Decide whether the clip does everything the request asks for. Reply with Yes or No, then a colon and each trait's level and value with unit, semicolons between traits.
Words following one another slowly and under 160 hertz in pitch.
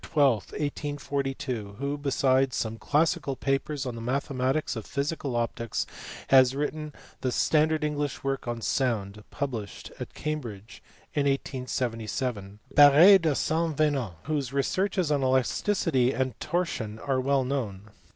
Yes: slow, 130 wpm; low, 135 Hz